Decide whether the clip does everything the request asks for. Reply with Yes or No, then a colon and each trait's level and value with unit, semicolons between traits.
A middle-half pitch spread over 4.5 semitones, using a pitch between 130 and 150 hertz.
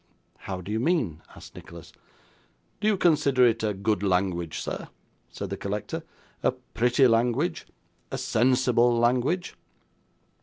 No: average, 4.9 semitones; low, 120 Hz